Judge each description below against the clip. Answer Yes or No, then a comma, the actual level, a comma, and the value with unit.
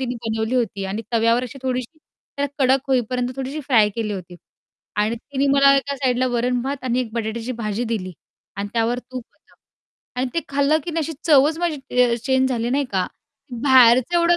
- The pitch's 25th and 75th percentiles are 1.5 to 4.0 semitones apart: Yes, average, 3.2 semitones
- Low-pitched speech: No, very high, 250 Hz